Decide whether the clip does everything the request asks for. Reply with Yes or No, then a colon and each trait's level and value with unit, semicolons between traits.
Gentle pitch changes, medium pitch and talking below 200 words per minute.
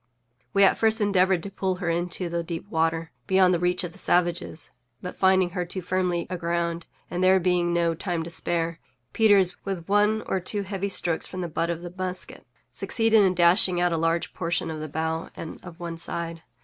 No: narrow, 2.0 semitones; medium, 175 Hz; fast, 205 wpm